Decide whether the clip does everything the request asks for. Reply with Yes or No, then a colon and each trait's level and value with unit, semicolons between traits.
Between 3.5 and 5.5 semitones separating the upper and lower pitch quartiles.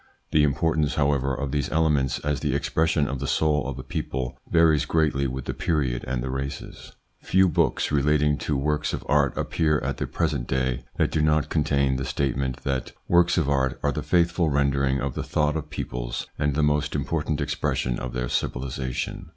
No: narrow, 2.5 semitones